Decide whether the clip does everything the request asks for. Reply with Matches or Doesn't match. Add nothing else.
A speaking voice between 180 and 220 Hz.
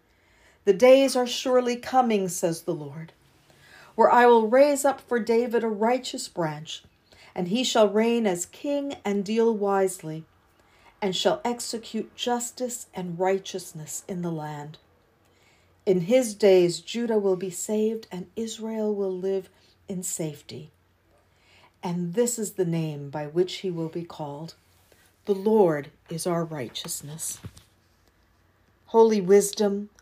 Matches